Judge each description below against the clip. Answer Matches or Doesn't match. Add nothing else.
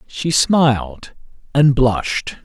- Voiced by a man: Matches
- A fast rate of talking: Doesn't match